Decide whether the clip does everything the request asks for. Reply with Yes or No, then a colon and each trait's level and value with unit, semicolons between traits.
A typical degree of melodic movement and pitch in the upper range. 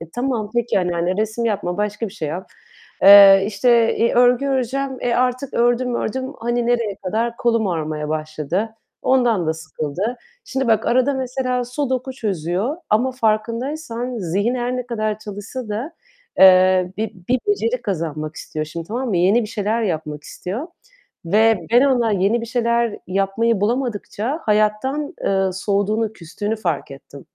Yes: average, 4.3 semitones; high, 220 Hz